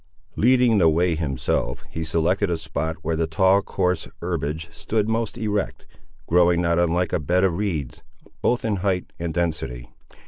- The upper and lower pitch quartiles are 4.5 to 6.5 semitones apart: No, average, 3.7 semitones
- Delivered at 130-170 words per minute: Yes, average, 165 wpm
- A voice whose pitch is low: Yes, very low, 85 Hz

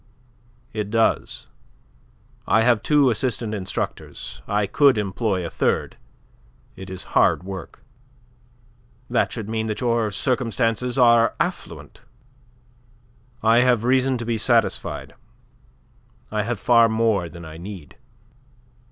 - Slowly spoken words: Yes, slow, 115 wpm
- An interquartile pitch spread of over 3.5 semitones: No, average, 2.9 semitones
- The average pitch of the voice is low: Yes, low, 115 Hz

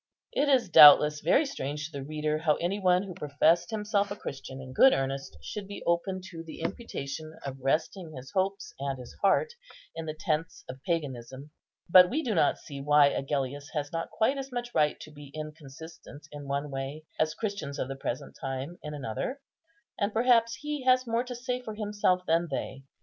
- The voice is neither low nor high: Yes, medium, 160 Hz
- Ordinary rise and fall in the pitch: No, wide, 6.4 semitones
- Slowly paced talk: No, average, 195 wpm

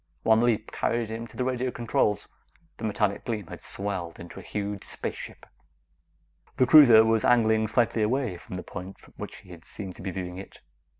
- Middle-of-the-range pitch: No, low, 110 Hz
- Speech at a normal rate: Yes, average, 185 wpm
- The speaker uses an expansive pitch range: No, average, 3.3 semitones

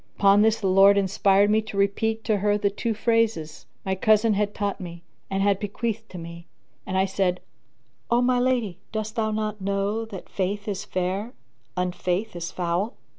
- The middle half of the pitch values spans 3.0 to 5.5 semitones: No, narrow, 2.4 semitones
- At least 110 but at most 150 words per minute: No, average, 180 wpm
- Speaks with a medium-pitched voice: No, high, 200 Hz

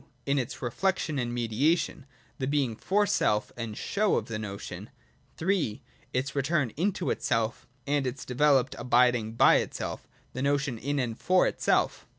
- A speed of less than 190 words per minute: Yes, average, 160 wpm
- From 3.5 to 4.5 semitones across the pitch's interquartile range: Yes, average, 3.9 semitones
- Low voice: Yes, low, 130 Hz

